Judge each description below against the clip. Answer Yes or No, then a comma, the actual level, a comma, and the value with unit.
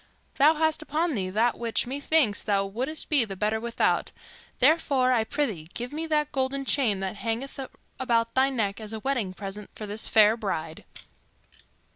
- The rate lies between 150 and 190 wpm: Yes, average, 170 wpm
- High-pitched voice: Yes, high, 235 Hz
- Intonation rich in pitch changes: No, average, 4.9 semitones